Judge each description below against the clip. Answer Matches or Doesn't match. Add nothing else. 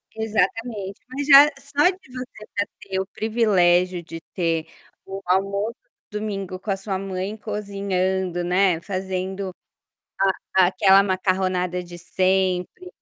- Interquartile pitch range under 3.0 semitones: Matches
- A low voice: Doesn't match